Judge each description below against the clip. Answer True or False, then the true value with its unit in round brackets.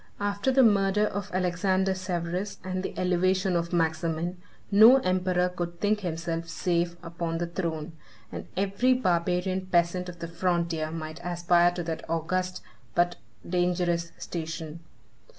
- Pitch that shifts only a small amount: True (1.8 semitones)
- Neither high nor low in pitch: True (175 Hz)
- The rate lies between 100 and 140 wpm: True (135 wpm)